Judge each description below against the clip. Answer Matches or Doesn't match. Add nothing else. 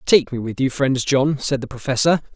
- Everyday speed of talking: Doesn't match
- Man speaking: Matches